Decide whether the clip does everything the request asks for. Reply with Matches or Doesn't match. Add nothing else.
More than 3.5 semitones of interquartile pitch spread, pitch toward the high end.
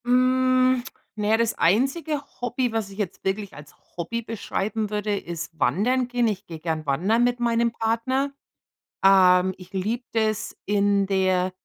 Matches